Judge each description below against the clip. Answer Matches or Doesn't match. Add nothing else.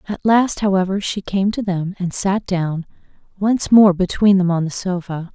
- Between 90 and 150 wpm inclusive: Doesn't match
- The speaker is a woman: Matches